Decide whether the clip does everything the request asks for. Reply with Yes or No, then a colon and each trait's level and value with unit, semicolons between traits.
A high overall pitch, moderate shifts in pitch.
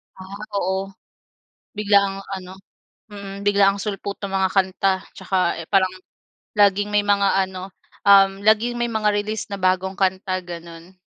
No: high, 195 Hz; narrow, 1.4 semitones